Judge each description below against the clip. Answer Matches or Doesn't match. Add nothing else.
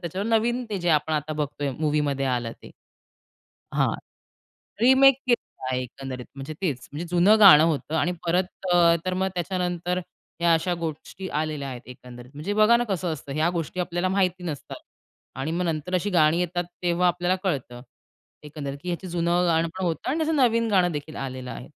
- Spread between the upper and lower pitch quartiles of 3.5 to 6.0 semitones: Matches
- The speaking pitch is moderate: Matches